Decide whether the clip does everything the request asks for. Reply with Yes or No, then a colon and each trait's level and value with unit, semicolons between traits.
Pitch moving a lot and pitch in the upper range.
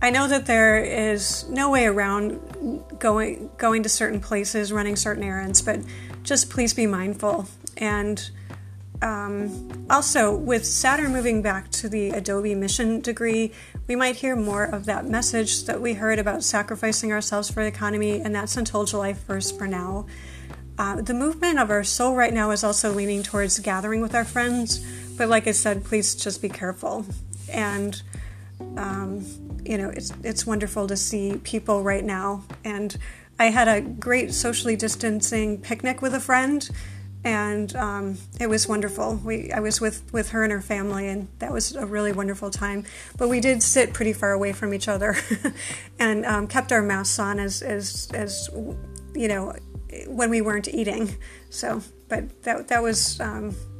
Yes: wide, 8.4 semitones; high, 210 Hz